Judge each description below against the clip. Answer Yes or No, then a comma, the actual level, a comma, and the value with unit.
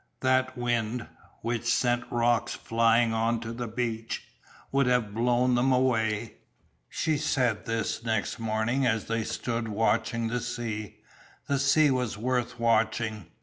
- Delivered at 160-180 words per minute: No, average, 140 wpm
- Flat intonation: Yes, narrow, 1.7 semitones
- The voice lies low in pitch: Yes, low, 115 Hz